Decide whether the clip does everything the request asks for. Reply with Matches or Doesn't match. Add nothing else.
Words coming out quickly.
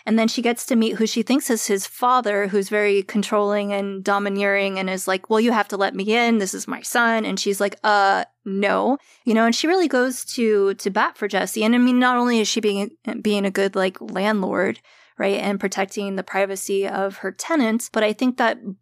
Matches